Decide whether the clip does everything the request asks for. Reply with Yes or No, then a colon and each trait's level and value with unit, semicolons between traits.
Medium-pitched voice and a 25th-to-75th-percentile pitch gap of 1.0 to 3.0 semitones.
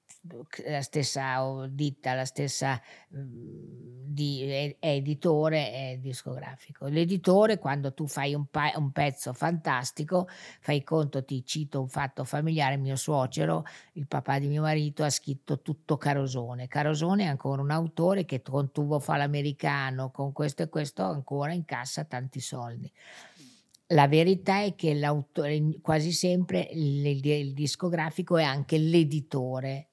Yes: medium, 145 Hz; narrow, 2.6 semitones